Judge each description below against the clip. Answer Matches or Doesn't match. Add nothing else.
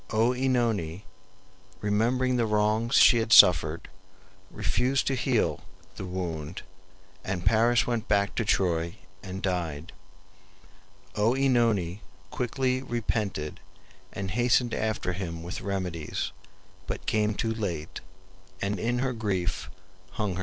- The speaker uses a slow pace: Matches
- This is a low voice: Matches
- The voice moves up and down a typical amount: Matches